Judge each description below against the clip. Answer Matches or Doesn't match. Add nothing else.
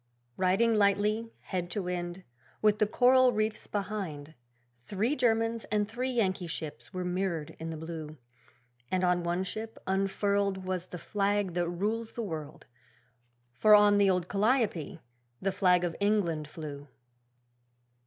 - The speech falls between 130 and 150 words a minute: Matches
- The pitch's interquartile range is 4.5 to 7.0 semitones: Doesn't match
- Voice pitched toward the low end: Doesn't match